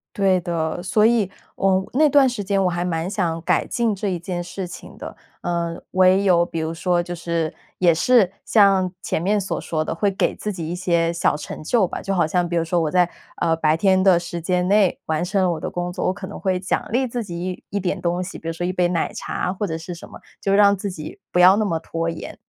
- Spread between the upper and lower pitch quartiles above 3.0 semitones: No, narrow, 2.4 semitones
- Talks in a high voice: No, medium, 180 Hz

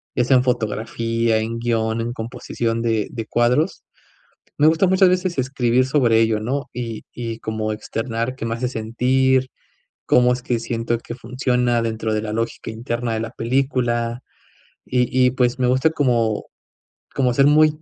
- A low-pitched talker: Yes, low, 120 Hz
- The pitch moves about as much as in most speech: No, narrow, 2.2 semitones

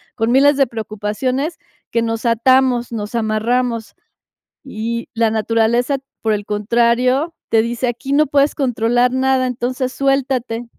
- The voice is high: Yes, high, 240 Hz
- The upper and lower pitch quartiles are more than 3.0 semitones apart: No, narrow, 2.5 semitones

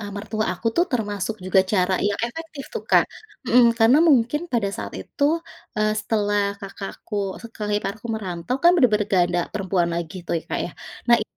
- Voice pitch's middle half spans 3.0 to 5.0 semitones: Yes, average, 3.3 semitones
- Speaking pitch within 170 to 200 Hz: No, high, 215 Hz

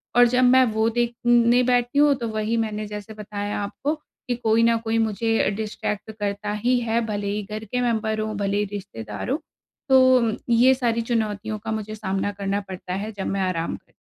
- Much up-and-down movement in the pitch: No, narrow, 2.6 semitones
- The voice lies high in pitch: Yes, high, 220 Hz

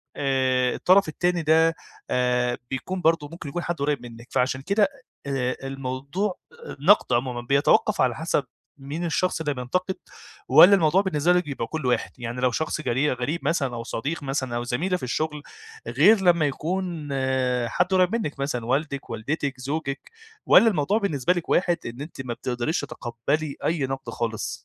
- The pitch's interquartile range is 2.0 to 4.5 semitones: No, average, 5.1 semitones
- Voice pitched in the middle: Yes, medium, 145 Hz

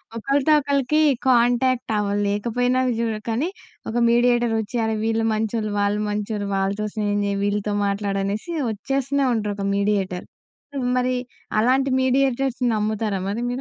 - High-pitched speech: Yes, high, 225 Hz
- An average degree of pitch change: Yes, average, 3.6 semitones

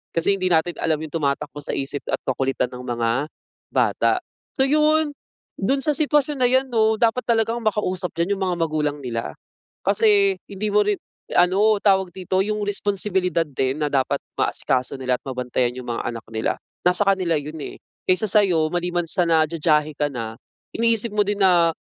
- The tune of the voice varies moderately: No, wide, 6.3 semitones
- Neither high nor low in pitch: Yes, medium, 180 Hz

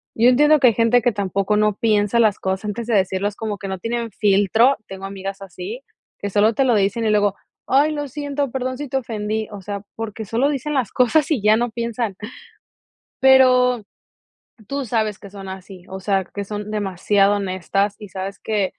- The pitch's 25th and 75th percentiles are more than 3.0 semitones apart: Yes, average, 3.7 semitones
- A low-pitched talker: No, high, 215 Hz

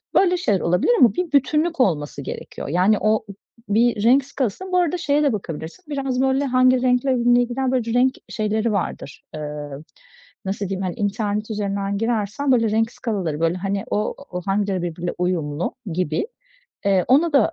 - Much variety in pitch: Yes, wide, 5.8 semitones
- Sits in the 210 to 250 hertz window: Yes, high, 215 Hz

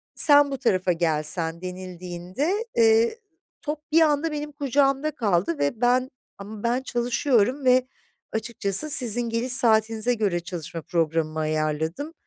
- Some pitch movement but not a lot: No, wide, 7.6 semitones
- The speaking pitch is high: Yes, high, 225 Hz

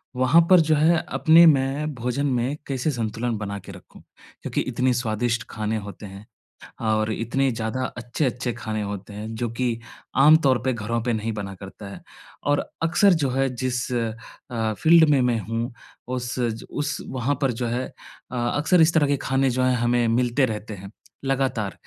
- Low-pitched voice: Yes, low, 125 Hz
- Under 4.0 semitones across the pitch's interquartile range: Yes, average, 3.4 semitones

